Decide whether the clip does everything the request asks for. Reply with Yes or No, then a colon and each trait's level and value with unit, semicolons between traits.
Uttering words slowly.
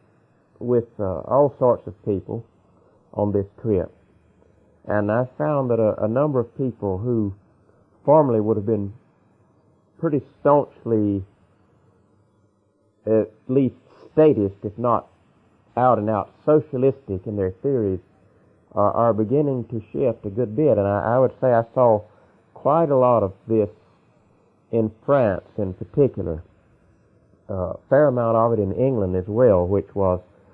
No: average, 145 wpm